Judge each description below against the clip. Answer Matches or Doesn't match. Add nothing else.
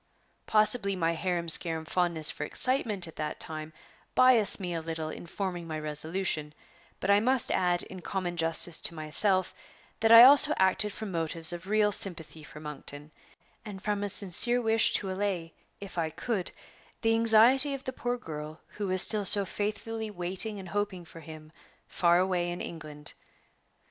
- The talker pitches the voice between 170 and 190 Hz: Matches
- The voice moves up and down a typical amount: Matches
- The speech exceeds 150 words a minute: Matches